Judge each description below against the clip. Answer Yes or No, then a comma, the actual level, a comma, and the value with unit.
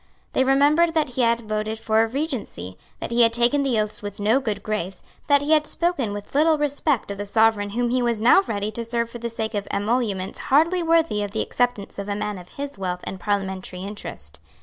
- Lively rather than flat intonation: No, average, 4.9 semitones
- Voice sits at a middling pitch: No, high, 225 Hz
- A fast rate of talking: Yes, fast, 225 wpm